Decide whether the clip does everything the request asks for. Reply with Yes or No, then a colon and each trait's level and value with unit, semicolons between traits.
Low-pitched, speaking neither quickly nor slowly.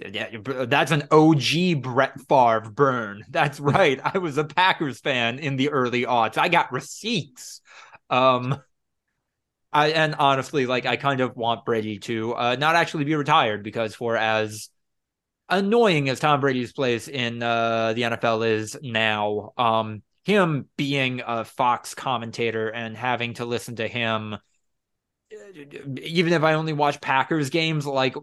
Yes: low, 130 Hz; average, 150 wpm